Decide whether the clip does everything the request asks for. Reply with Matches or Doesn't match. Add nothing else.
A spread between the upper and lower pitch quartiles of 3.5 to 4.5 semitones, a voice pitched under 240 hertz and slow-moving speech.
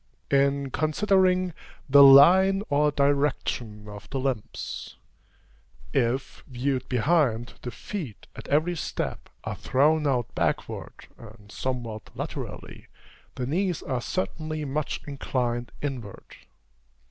Matches